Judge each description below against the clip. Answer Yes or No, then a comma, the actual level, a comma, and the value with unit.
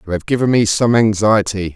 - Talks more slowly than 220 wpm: Yes, fast, 205 wpm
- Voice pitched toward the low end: Yes, low, 105 Hz